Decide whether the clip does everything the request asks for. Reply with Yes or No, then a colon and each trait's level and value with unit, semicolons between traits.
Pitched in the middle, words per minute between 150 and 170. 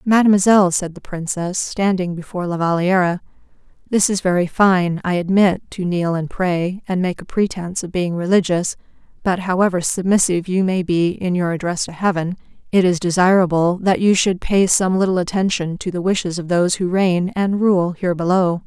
No: medium, 180 Hz; average, 185 wpm